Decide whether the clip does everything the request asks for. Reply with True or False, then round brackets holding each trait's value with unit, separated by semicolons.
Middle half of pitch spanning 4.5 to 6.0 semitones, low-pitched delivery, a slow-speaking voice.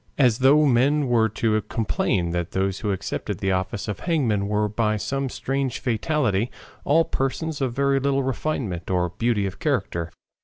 False (5.6 semitones; 115 Hz; 165 wpm)